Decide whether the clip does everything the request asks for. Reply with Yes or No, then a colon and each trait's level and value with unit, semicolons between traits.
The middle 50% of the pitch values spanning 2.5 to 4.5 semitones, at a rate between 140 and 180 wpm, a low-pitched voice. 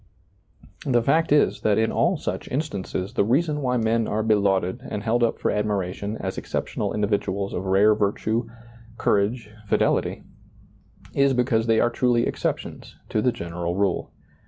Yes: average, 3.3 semitones; average, 155 wpm; low, 110 Hz